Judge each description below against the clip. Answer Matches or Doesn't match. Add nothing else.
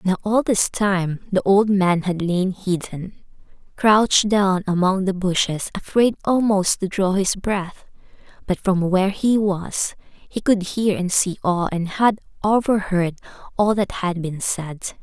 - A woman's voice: Matches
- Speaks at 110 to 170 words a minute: Matches